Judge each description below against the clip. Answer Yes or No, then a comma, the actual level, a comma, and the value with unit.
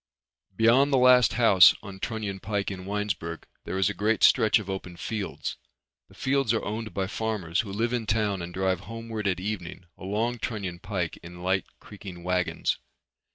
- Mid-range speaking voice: No, low, 100 Hz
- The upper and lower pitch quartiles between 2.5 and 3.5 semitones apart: Yes, average, 3.2 semitones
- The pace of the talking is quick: No, average, 175 wpm